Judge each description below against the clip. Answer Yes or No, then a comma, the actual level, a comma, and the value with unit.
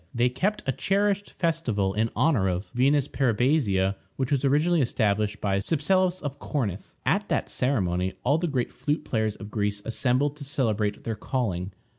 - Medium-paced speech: Yes, average, 165 wpm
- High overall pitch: No, low, 125 Hz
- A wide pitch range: Yes, wide, 6.0 semitones